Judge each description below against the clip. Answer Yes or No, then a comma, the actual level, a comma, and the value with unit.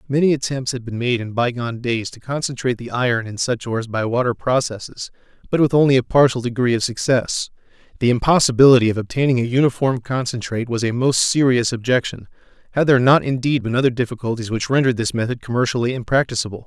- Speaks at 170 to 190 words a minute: Yes, average, 185 wpm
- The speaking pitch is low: Yes, low, 125 Hz